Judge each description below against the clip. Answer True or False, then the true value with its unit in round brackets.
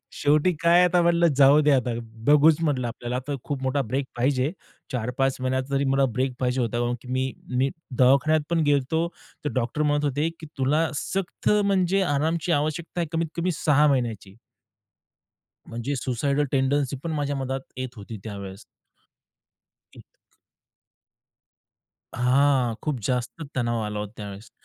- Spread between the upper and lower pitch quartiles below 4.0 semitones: True (3.3 semitones)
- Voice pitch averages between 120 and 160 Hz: True (135 Hz)